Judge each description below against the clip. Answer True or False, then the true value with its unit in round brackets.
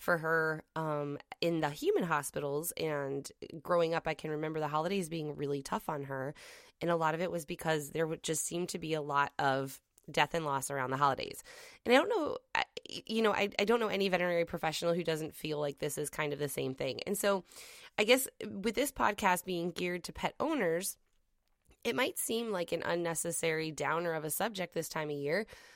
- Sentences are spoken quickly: True (210 wpm)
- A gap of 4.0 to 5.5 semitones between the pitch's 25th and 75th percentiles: True (4.5 semitones)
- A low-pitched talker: False (165 Hz)